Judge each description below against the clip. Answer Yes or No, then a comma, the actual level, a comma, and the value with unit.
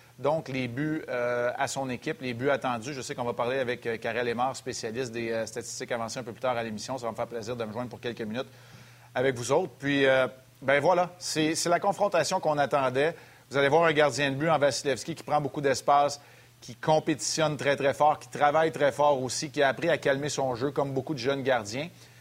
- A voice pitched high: No, low, 135 Hz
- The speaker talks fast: Yes, fast, 240 wpm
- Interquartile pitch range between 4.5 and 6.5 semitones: No, average, 3.2 semitones